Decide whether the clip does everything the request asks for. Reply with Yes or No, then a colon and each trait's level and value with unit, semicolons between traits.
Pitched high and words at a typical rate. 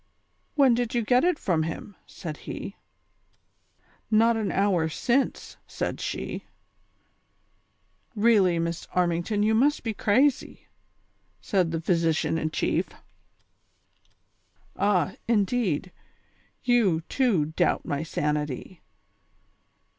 No: high, 195 Hz; slow, 115 wpm